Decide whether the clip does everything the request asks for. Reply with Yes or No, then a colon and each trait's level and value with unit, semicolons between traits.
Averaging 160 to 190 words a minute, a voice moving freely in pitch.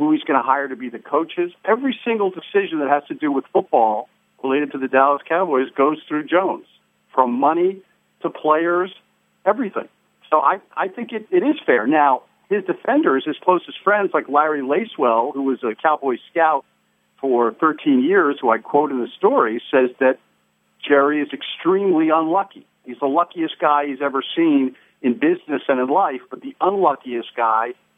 Yes: average, 180 wpm; wide, 7.1 semitones